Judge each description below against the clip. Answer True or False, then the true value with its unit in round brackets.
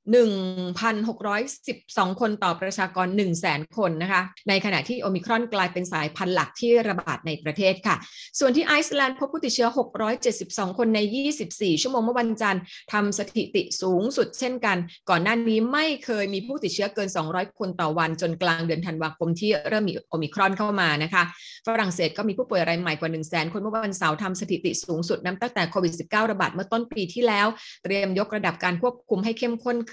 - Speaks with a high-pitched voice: True (200 Hz)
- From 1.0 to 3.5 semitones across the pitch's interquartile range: False (4.2 semitones)